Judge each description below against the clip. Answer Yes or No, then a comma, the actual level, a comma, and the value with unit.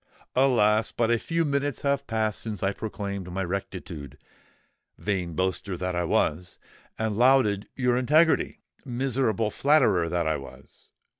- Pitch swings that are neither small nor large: No, wide, 5.8 semitones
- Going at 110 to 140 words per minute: Yes, slow, 135 wpm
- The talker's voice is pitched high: No, low, 105 Hz